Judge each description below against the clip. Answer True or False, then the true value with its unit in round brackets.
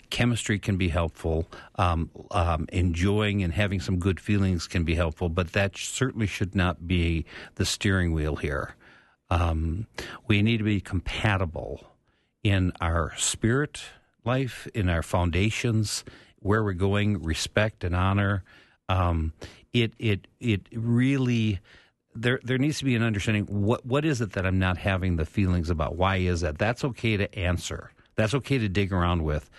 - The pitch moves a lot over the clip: False (3.8 semitones)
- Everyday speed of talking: True (165 wpm)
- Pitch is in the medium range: False (100 Hz)